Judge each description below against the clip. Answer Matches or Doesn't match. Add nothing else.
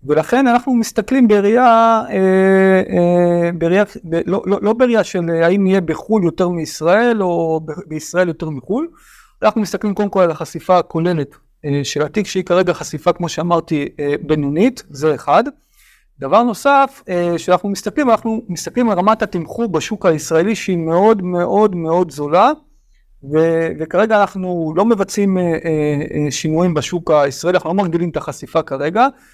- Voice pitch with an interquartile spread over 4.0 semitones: Matches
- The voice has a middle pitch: Matches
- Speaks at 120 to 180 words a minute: Matches